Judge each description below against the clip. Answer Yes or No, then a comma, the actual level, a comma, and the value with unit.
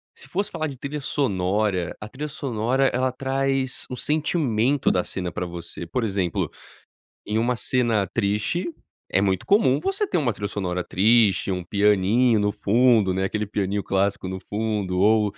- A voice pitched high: No, low, 110 Hz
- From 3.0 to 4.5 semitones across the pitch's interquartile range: No, average, 5.1 semitones